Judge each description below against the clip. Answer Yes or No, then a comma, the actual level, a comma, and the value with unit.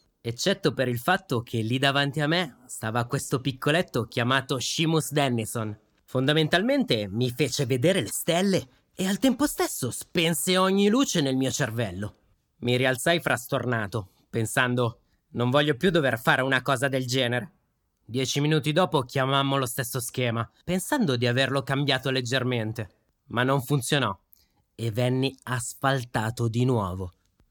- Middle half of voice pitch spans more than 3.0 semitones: Yes, average, 4.1 semitones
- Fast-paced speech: No, average, 140 wpm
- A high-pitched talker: No, low, 130 Hz